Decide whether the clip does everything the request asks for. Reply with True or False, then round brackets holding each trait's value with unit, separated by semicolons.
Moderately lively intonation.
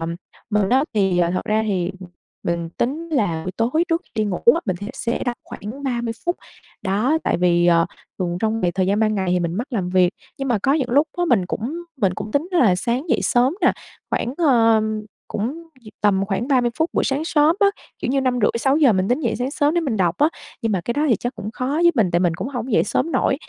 False (6.3 semitones)